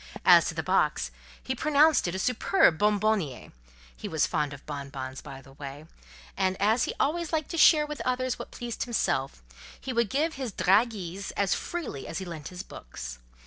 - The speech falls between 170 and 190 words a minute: Yes, average, 180 wpm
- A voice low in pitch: No, high, 190 Hz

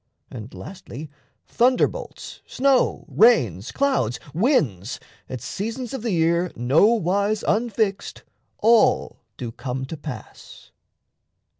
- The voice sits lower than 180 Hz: No, medium, 185 Hz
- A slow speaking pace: Yes, slow, 105 wpm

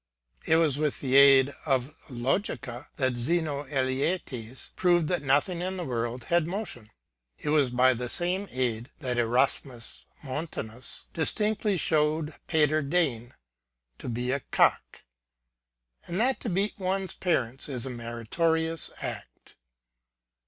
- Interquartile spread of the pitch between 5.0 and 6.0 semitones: Yes, wide, 5.4 semitones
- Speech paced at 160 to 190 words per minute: No, slow, 135 wpm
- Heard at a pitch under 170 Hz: Yes, medium, 140 Hz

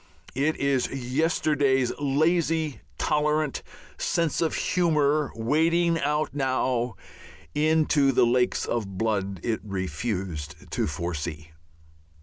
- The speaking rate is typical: No, slow, 100 wpm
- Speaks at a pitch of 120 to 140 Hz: Yes, low, 135 Hz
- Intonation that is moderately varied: No, wide, 5.7 semitones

